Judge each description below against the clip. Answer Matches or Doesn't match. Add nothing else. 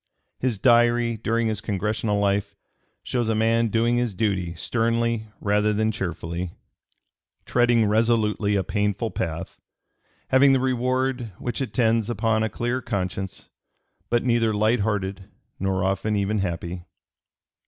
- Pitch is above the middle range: Doesn't match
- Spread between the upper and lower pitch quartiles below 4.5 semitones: Matches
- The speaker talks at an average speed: Doesn't match